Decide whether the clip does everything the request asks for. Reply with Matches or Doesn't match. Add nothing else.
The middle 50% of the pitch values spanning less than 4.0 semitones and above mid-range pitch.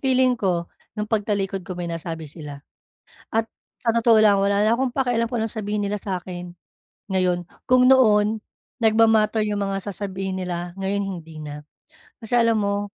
Matches